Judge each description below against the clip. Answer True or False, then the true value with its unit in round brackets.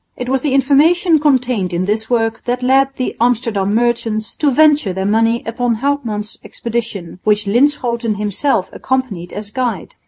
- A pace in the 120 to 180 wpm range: True (155 wpm)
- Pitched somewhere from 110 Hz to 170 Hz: False (235 Hz)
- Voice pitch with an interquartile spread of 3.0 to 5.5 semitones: True (3.9 semitones)